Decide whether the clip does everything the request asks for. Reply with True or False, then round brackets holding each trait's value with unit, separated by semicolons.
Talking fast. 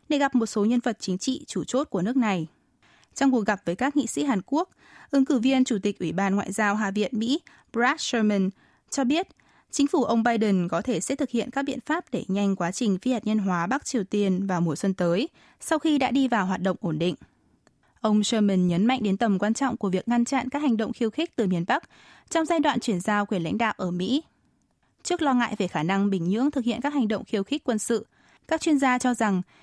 True (255 wpm)